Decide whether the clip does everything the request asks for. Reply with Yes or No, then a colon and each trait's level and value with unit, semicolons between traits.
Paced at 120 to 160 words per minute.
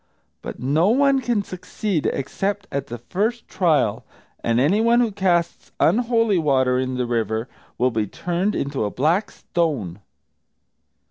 Yes: average, 140 wpm